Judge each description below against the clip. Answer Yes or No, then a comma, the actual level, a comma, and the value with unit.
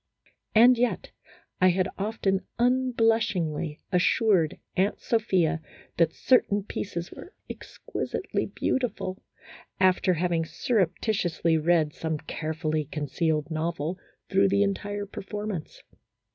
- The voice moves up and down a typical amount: Yes, average, 4.3 semitones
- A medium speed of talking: No, slow, 105 wpm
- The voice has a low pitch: No, medium, 185 Hz